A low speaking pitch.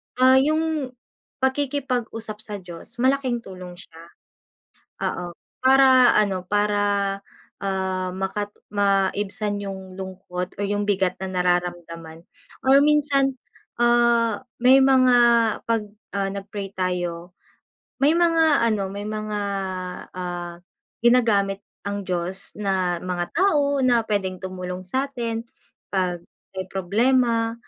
No: high, 205 Hz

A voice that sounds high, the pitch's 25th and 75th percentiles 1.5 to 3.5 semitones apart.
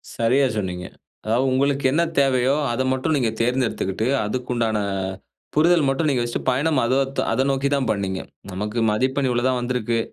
No: low, 130 Hz; average, 2.9 semitones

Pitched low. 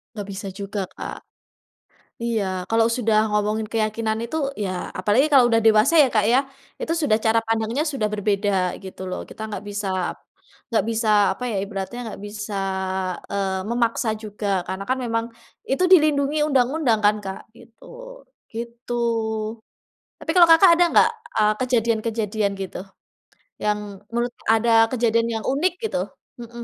No: high, 225 Hz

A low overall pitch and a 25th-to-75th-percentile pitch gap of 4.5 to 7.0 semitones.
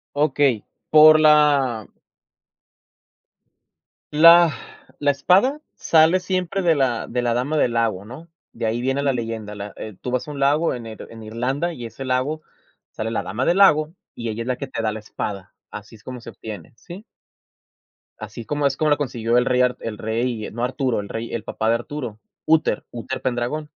Yes: low, 125 Hz; average, 4.8 semitones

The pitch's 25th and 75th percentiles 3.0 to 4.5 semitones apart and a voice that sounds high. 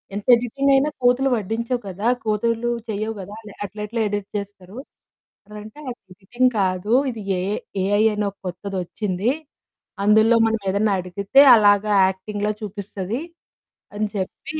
No: narrow, 2.4 semitones; high, 210 Hz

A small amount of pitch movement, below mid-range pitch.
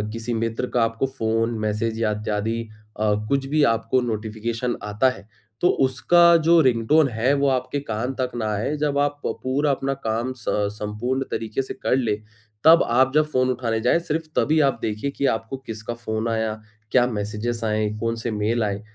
No: average, 3.5 semitones; low, 120 Hz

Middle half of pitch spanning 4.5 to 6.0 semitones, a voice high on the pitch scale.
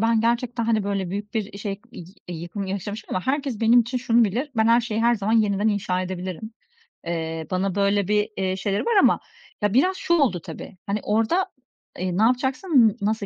No: average, 3.4 semitones; high, 210 Hz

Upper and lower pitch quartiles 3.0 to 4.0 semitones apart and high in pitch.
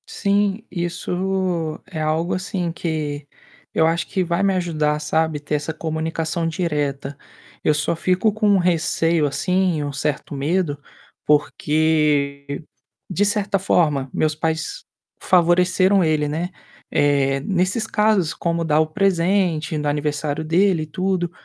No: average, 3.6 semitones; medium, 165 Hz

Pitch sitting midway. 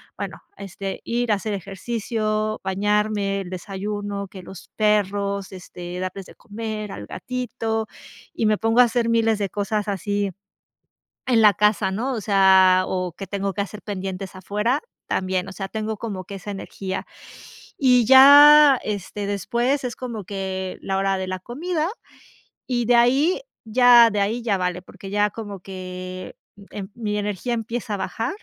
No: high, 205 Hz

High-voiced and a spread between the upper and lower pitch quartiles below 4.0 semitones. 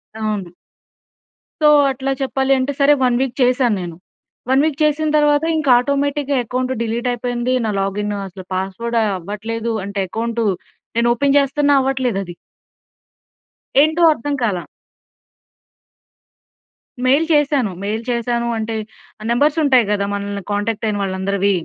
No: high, 240 Hz; average, 5.1 semitones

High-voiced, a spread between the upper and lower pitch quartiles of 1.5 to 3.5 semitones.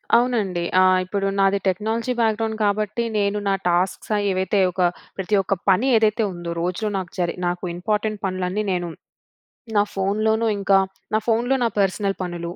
Yes: high, 200 Hz; average, 2.9 semitones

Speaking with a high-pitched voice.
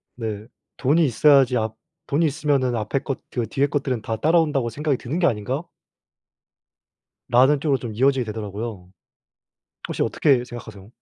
No: low, 130 Hz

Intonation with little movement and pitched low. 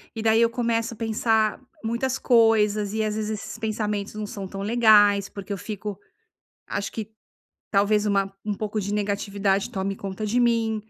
No: narrow, 1.7 semitones; high, 210 Hz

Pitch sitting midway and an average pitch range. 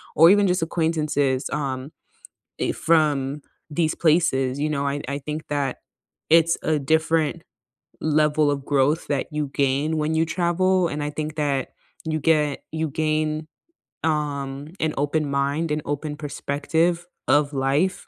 No: medium, 150 Hz; narrow, 2.1 semitones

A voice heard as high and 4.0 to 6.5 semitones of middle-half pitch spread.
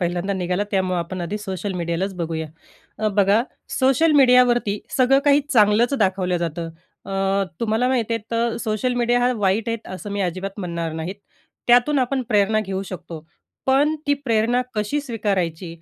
Yes: high, 210 Hz; average, 4.8 semitones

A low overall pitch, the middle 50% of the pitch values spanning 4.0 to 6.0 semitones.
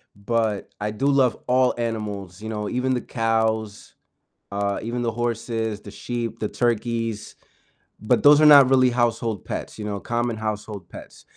No: low, 115 Hz; narrow, 2.4 semitones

